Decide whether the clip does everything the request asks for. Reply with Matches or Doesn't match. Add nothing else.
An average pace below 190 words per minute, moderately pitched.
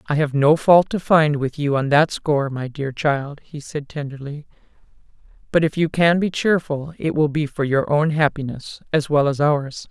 Doesn't match